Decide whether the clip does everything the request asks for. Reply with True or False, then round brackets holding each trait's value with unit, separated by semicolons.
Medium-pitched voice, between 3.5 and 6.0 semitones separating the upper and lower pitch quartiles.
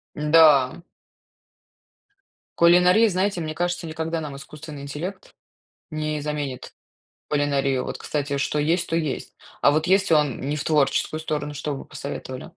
False (155 Hz; 2.5 semitones)